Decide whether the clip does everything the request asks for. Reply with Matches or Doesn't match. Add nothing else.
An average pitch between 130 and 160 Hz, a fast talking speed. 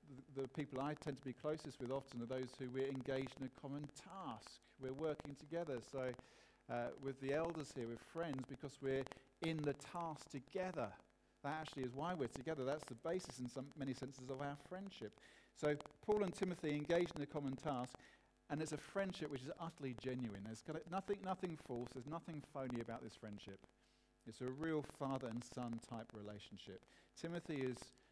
Doesn't match